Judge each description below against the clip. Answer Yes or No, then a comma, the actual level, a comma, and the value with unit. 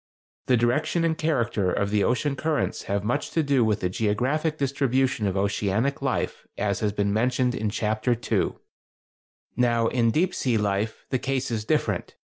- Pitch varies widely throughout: No, average, 4.5 semitones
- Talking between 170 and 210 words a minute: Yes, average, 180 wpm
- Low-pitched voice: Yes, low, 120 Hz